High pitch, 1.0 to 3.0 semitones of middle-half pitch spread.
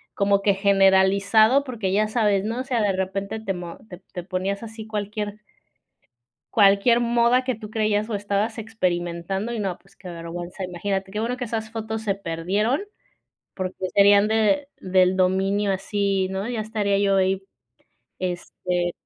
Yes: high, 200 Hz; narrow, 2.5 semitones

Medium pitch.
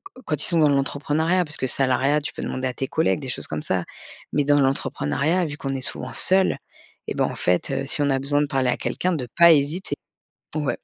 Yes: medium, 145 Hz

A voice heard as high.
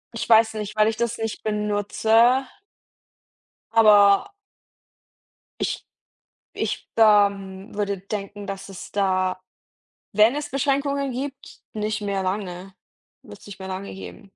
Yes: high, 210 Hz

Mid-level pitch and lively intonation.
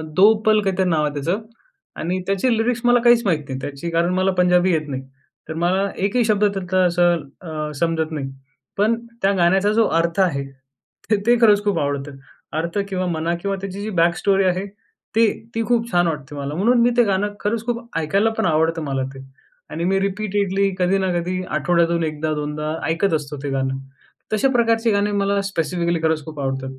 No: medium, 180 Hz; average, 4.3 semitones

